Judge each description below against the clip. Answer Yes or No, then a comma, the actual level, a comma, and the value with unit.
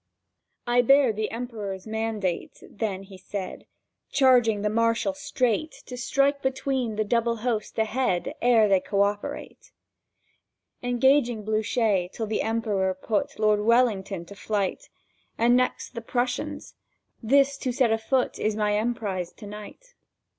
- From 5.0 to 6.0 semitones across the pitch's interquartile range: No, average, 3.1 semitones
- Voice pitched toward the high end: Yes, high, 225 Hz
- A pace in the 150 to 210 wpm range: No, slow, 135 wpm